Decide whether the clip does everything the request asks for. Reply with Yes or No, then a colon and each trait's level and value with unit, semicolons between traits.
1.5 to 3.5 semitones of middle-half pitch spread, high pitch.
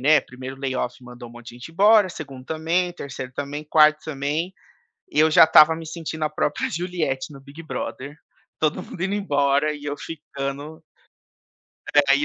No: average, 2.7 semitones; medium, 150 Hz